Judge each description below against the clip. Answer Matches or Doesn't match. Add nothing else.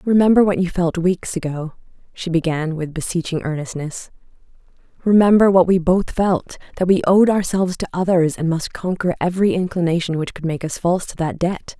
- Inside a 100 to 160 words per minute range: Doesn't match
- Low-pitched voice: Doesn't match